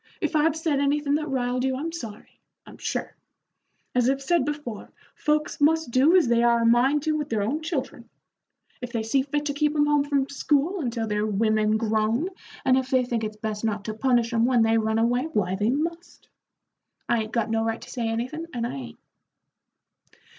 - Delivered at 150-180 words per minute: No, fast, 205 wpm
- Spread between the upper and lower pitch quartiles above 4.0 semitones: Yes, average, 4.7 semitones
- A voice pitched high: Yes, very high, 250 Hz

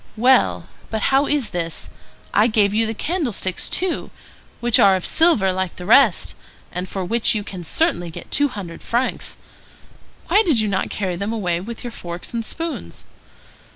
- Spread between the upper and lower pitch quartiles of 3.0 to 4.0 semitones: No, wide, 5.5 semitones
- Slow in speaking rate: No, average, 175 wpm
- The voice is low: No, high, 215 Hz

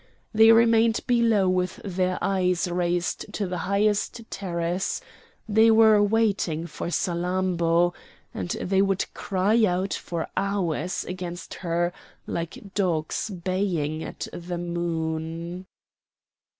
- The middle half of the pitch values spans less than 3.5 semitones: Yes, average, 2.7 semitones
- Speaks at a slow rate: Yes, slow, 110 wpm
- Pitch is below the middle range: No, medium, 185 Hz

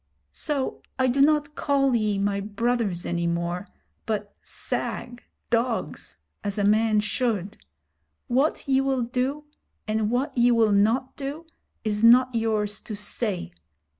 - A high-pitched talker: Yes, high, 230 Hz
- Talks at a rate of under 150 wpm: Yes, slow, 135 wpm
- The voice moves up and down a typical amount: Yes, average, 4.0 semitones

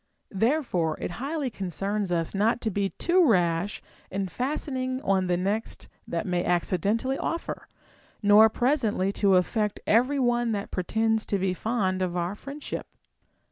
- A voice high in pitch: Yes, high, 210 Hz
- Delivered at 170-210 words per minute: No, average, 150 wpm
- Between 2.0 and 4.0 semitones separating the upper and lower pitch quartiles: No, average, 4.7 semitones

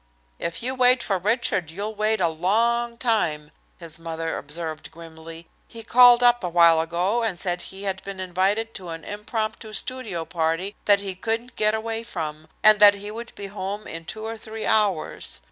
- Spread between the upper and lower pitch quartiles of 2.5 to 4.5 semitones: No, average, 4.9 semitones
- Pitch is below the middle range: No, high, 200 Hz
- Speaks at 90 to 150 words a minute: No, average, 185 wpm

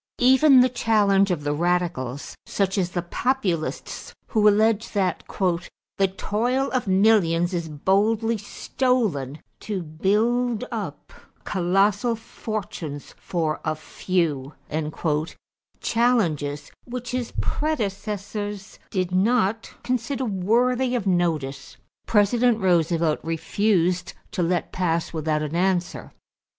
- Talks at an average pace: No, slow, 110 wpm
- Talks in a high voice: Yes, high, 195 Hz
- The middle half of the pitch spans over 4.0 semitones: Yes, average, 5.0 semitones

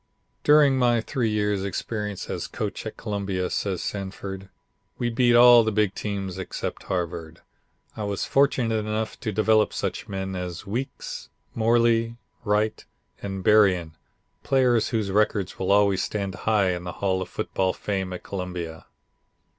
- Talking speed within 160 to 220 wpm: No, average, 145 wpm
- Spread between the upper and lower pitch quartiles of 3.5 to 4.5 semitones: No, average, 2.9 semitones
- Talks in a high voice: No, low, 105 Hz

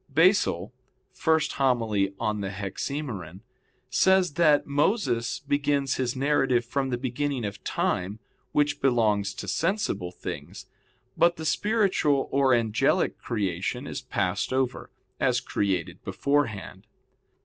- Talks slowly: Yes, slow, 115 wpm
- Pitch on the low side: Yes, low, 130 Hz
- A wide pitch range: Yes, wide, 6.0 semitones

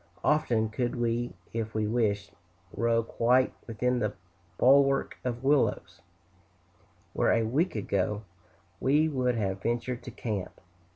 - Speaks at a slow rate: Yes, slow, 125 wpm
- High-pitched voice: No, low, 120 Hz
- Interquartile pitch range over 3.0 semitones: No, average, 2.7 semitones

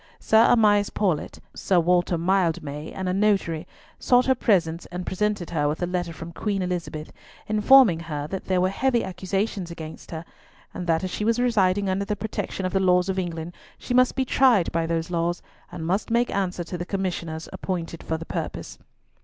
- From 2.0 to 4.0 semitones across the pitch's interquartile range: Yes, average, 3.5 semitones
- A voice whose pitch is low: No, medium, 185 Hz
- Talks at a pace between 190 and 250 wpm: Yes, average, 195 wpm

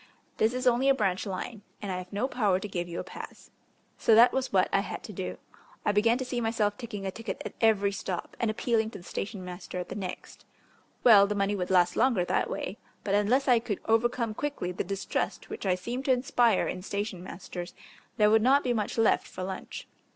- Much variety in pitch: No, average, 3.9 semitones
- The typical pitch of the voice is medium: No, high, 210 Hz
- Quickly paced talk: Yes, fast, 225 wpm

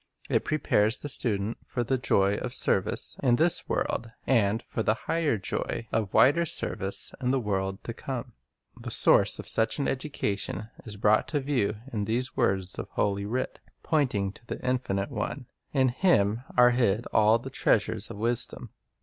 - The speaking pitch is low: Yes, low, 115 Hz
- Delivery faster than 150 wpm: Yes, average, 175 wpm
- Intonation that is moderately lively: Yes, average, 4.1 semitones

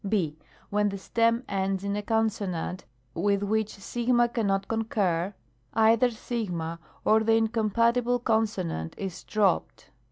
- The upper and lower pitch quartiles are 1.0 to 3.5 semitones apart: Yes, narrow, 2.5 semitones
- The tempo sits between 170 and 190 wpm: No, slow, 135 wpm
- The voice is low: No, high, 215 Hz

